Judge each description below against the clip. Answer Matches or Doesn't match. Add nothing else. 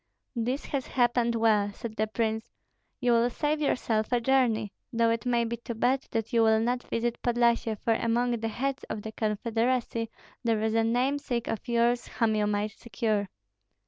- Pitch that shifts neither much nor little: Doesn't match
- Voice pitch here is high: Matches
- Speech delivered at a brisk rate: Doesn't match